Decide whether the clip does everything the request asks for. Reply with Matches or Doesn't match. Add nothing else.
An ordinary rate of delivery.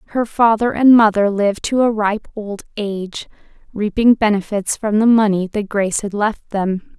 Matches